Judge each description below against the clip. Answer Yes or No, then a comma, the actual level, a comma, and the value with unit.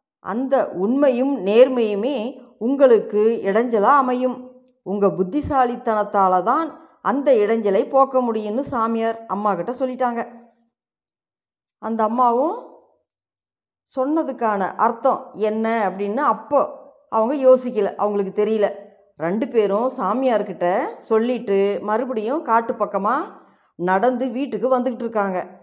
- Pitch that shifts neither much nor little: Yes, average, 4.0 semitones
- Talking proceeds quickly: No, average, 90 wpm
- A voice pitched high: Yes, high, 230 Hz